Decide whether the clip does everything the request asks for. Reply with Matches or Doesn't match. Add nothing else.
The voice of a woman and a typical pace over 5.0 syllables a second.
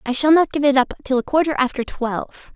Matches